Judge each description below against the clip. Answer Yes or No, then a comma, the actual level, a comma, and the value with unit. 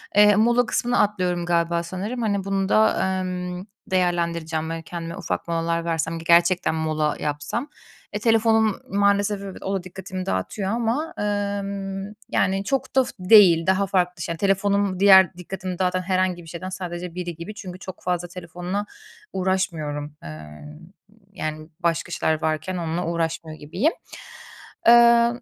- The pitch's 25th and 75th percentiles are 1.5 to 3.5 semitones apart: Yes, average, 3.0 semitones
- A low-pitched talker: No, medium, 185 Hz